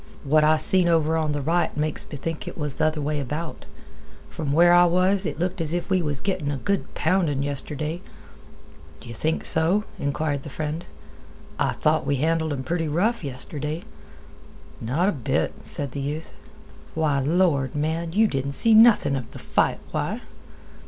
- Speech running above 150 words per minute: Yes, average, 180 wpm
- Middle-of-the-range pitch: Yes, medium, 155 Hz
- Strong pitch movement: No, average, 3.2 semitones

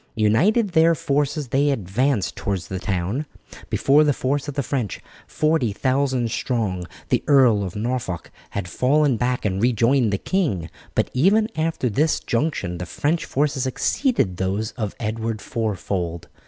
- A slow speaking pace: No, average, 145 wpm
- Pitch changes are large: Yes, wide, 6.2 semitones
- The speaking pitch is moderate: No, low, 125 Hz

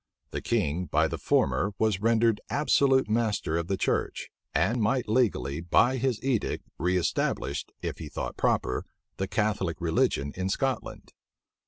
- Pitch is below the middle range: Yes, low, 105 Hz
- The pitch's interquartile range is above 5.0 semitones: Yes, wide, 5.6 semitones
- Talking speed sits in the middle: Yes, average, 145 wpm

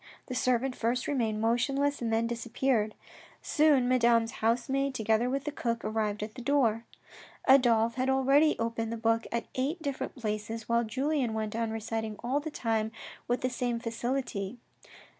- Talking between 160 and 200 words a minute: Yes, average, 165 wpm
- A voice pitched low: No, high, 235 Hz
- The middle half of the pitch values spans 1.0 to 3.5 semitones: Yes, average, 2.9 semitones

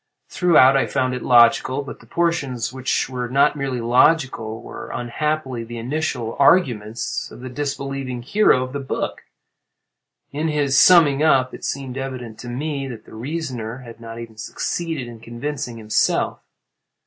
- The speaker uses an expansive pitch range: No, average, 3.3 semitones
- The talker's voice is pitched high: No, low, 130 Hz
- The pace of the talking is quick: No, average, 155 wpm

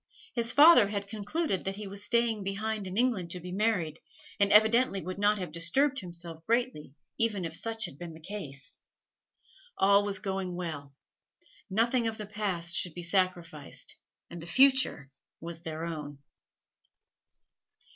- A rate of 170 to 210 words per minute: No, average, 155 wpm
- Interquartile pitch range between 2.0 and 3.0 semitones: No, average, 4.4 semitones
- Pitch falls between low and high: No, high, 195 Hz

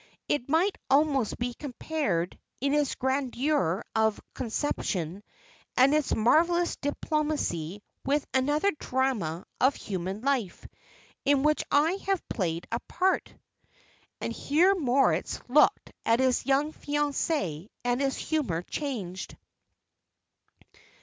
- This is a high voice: Yes, very high, 270 Hz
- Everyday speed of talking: No, slow, 110 wpm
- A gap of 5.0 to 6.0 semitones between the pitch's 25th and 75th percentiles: Yes, wide, 5.4 semitones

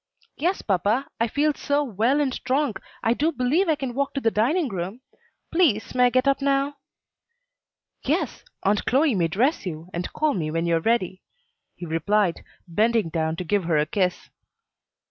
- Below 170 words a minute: No, average, 185 wpm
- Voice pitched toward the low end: No, high, 230 Hz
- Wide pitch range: Yes, wide, 7.5 semitones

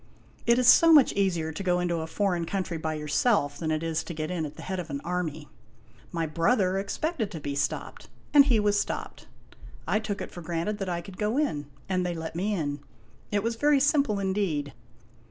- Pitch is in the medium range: Yes, medium, 180 Hz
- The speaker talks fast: Yes, fast, 215 wpm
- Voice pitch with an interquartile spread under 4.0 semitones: No, average, 4.7 semitones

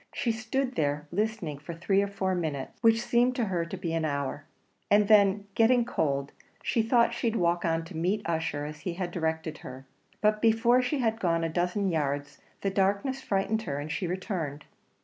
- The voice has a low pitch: No, medium, 185 Hz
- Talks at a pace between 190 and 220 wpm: Yes, average, 195 wpm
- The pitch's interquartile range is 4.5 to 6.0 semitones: Yes, wide, 5.6 semitones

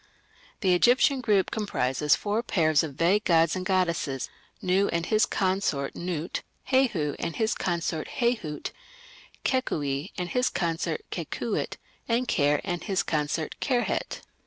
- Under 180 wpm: Yes, slow, 135 wpm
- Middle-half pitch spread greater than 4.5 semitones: Yes, average, 5.3 semitones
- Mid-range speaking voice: Yes, medium, 180 Hz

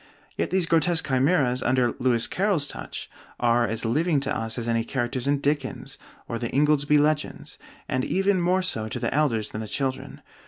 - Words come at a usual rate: Yes, average, 185 wpm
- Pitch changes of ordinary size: Yes, average, 4.3 semitones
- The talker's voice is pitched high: No, low, 135 Hz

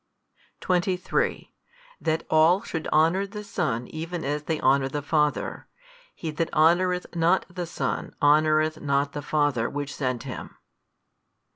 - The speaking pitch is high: No, medium, 155 Hz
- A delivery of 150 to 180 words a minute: No, slow, 135 wpm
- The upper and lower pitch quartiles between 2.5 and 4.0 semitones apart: Yes, average, 3.2 semitones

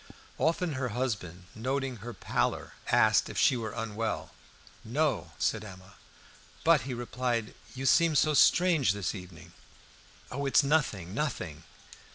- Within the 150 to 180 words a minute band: No, slow, 135 wpm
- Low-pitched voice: Yes, low, 120 Hz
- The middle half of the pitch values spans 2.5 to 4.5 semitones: No, average, 5.1 semitones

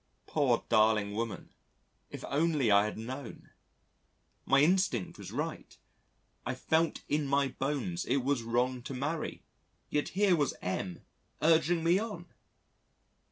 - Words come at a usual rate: No, slow, 130 wpm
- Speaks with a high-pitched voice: No, medium, 140 Hz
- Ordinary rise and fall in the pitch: No, wide, 5.8 semitones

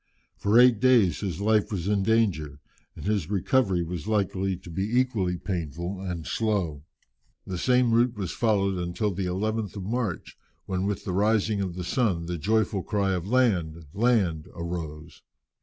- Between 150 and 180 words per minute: Yes, average, 165 wpm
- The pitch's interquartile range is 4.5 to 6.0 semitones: No, average, 3.9 semitones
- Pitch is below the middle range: Yes, very low, 95 Hz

